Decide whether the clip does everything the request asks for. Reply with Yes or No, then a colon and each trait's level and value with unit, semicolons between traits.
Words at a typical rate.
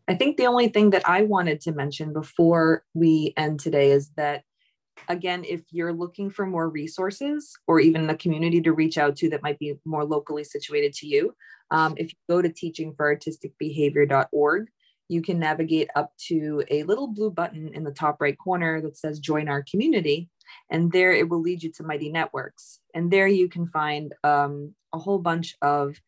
Yes: average, 190 wpm